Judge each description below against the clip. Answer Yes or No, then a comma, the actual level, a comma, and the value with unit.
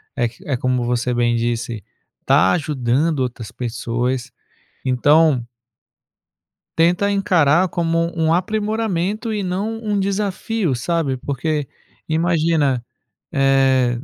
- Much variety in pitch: Yes, wide, 6.2 semitones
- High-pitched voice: No, medium, 150 Hz